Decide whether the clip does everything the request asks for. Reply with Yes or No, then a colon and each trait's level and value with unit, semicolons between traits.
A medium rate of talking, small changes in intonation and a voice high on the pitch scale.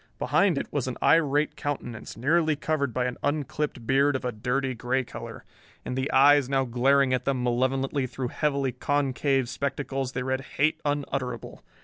No: average, 165 wpm; narrow, 2.2 semitones; low, 135 Hz